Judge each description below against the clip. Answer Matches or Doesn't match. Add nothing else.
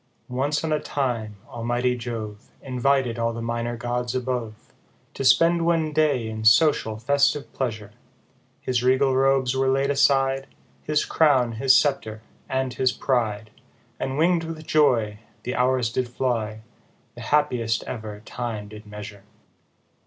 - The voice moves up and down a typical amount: Matches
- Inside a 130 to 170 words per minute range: Matches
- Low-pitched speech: Matches